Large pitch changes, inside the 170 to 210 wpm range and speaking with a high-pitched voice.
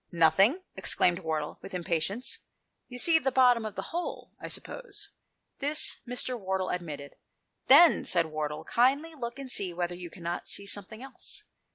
Yes: wide, 7.1 semitones; average, 175 wpm; high, 200 Hz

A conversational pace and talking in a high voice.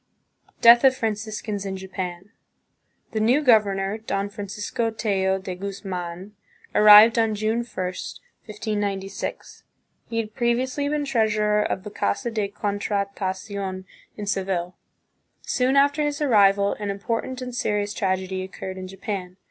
No: slow, 130 wpm; high, 205 Hz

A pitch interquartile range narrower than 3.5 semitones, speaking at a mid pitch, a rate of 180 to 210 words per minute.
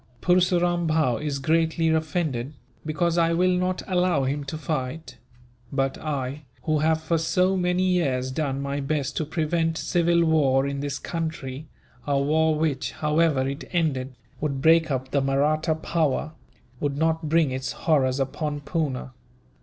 No: average, 3.1 semitones; medium, 155 Hz; average, 155 wpm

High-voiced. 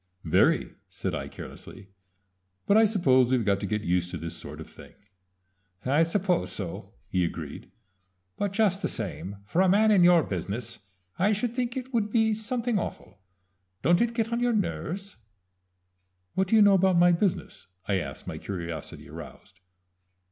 No: medium, 175 Hz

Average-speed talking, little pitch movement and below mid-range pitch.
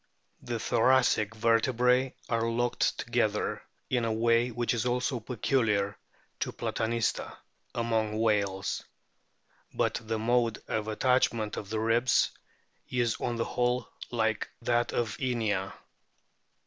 No: slow, 120 wpm; narrow, 1.9 semitones; low, 115 Hz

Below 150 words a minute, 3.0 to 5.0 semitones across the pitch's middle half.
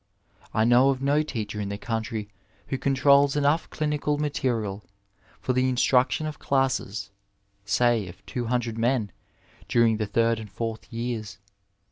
Yes: average, 140 wpm; average, 3.8 semitones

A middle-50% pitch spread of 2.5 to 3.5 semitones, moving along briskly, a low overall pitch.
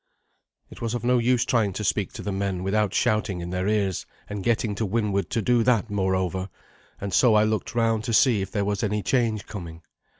Yes: average, 2.9 semitones; fast, 220 wpm; low, 105 Hz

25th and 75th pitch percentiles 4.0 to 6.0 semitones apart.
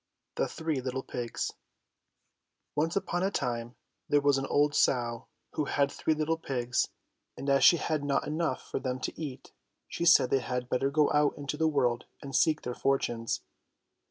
No: average, 3.3 semitones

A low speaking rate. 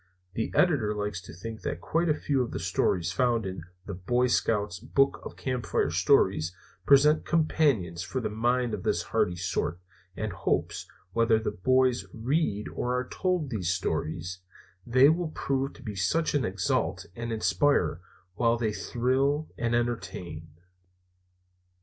No: average, 150 wpm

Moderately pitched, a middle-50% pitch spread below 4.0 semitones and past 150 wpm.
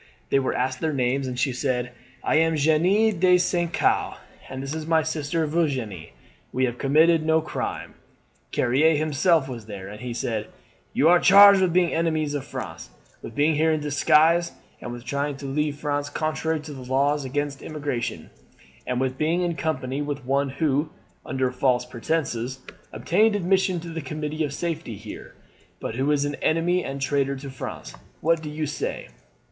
Yes: medium, 145 Hz; average, 3.5 semitones; average, 180 wpm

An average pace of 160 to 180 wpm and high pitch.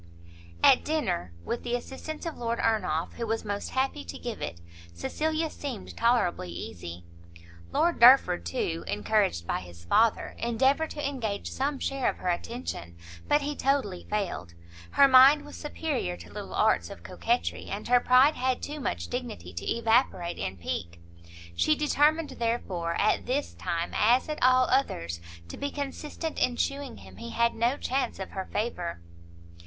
Yes: average, 165 wpm; high, 235 Hz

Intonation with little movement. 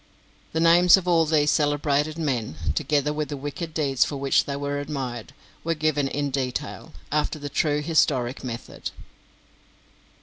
Yes: narrow, 2.2 semitones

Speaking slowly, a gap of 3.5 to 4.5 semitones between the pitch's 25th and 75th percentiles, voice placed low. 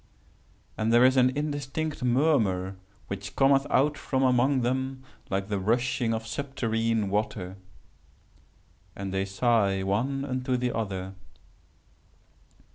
No: slow, 120 wpm; average, 5.0 semitones; low, 120 Hz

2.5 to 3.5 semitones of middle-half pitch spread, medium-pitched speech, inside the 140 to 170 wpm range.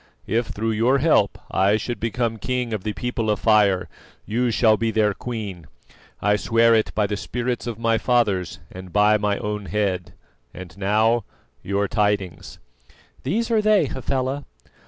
No: average, 2.9 semitones; low, 110 Hz; average, 160 wpm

